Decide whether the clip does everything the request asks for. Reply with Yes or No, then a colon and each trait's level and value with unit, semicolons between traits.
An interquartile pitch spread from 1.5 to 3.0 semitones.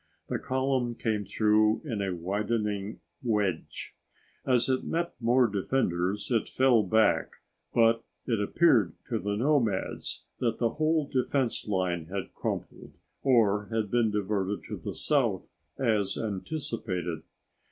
No: average, 3.9 semitones